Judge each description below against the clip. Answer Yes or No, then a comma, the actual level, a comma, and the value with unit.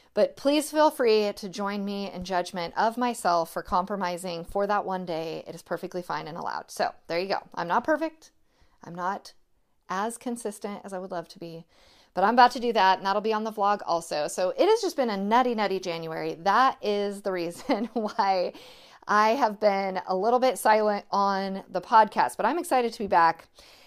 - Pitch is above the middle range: Yes, high, 200 Hz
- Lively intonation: No, average, 4.1 semitones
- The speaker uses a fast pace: Yes, fast, 210 wpm